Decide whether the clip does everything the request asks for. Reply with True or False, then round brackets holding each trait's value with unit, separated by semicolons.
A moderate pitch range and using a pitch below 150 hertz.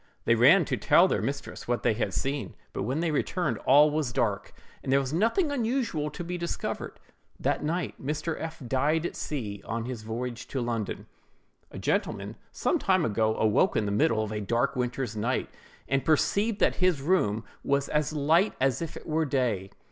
False (5.7 semitones; 135 Hz)